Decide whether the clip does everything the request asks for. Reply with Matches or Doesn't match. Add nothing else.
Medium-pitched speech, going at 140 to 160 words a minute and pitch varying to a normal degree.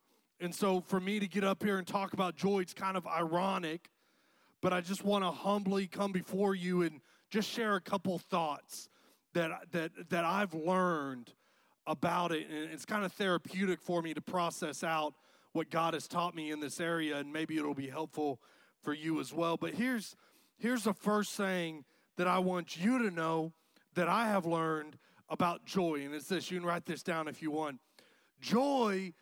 Doesn't match